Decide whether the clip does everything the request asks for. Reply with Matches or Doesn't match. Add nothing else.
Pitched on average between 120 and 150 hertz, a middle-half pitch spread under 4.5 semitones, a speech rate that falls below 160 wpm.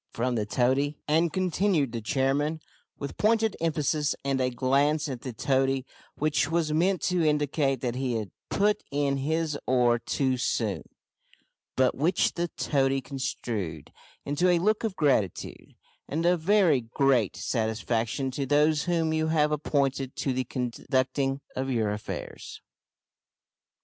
Matches